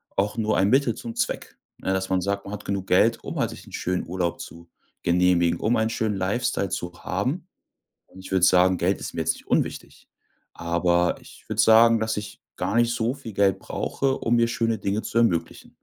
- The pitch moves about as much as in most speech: Yes, average, 3.9 semitones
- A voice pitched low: Yes, low, 100 Hz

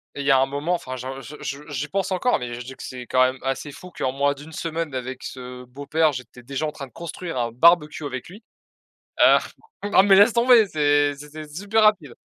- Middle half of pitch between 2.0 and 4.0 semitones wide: No, average, 4.5 semitones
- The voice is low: No, medium, 145 Hz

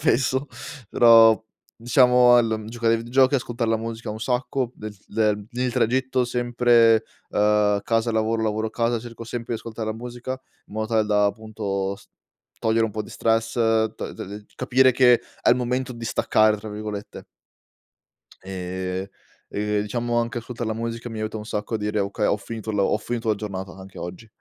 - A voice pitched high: No, low, 115 Hz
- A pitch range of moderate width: No, narrow, 2.2 semitones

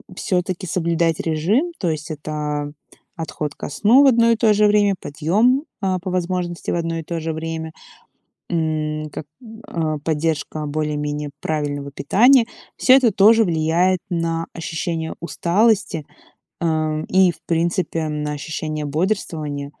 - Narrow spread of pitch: No, average, 3.5 semitones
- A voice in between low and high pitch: Yes, medium, 165 Hz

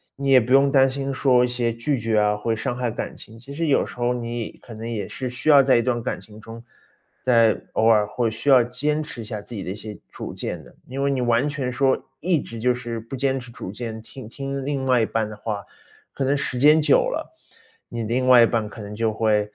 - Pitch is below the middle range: Yes, low, 120 Hz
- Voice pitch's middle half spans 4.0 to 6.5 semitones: No, average, 3.2 semitones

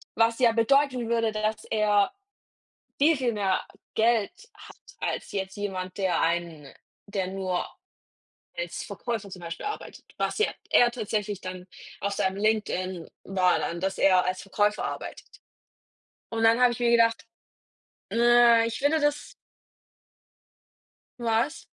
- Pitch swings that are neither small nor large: Yes, average, 3.8 semitones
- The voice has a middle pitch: No, high, 215 Hz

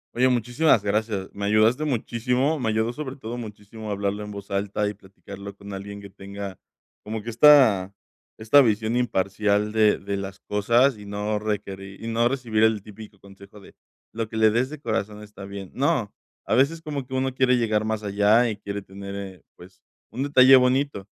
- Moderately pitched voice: No, low, 110 Hz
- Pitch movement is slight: No, average, 3.4 semitones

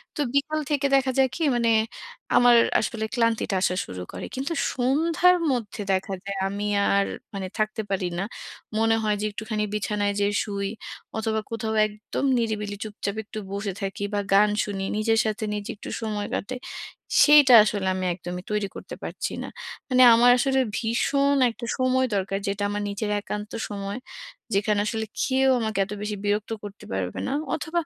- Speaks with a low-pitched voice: No, high, 215 Hz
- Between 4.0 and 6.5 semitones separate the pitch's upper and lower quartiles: No, average, 3.4 semitones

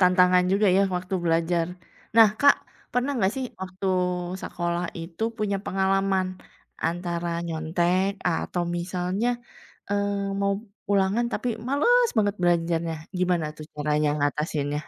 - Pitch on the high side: No, medium, 180 Hz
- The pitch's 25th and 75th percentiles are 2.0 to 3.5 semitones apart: Yes, average, 2.9 semitones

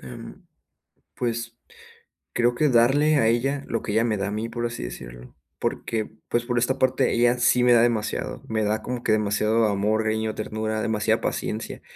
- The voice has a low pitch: Yes, low, 115 Hz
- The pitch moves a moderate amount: No, narrow, 1.9 semitones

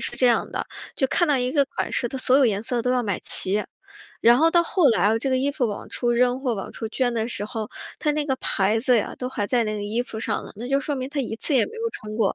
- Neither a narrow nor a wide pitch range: Yes, average, 3.5 semitones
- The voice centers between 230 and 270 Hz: Yes, high, 245 Hz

